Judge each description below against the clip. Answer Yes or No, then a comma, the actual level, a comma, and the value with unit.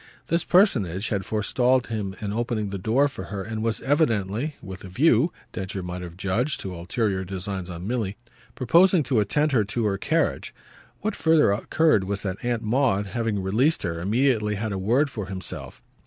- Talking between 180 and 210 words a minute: Yes, average, 185 wpm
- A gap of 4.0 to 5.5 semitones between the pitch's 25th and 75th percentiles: Yes, average, 4.9 semitones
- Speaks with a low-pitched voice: Yes, low, 110 Hz